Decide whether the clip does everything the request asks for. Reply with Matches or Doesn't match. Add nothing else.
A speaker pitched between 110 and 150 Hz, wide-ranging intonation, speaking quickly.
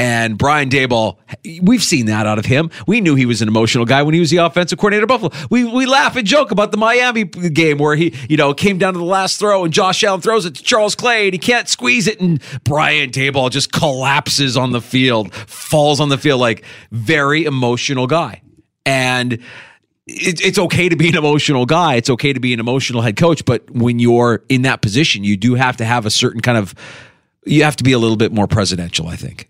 Matches